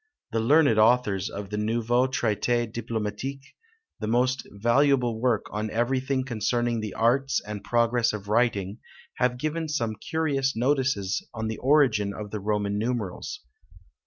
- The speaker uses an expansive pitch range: No, average, 3.4 semitones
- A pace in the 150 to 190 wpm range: No, average, 140 wpm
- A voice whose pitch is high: No, low, 115 Hz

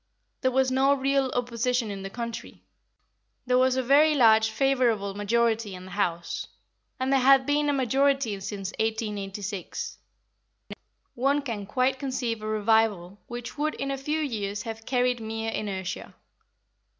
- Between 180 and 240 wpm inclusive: No, average, 150 wpm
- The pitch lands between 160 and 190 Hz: No, high, 235 Hz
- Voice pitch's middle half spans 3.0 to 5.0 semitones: Yes, average, 4.1 semitones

